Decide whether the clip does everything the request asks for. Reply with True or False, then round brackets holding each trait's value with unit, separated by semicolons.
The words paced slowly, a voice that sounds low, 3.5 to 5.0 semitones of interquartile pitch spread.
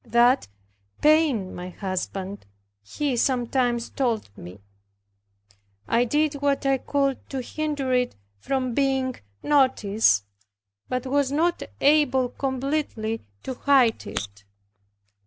False (105 wpm; 255 Hz; 3.9 semitones)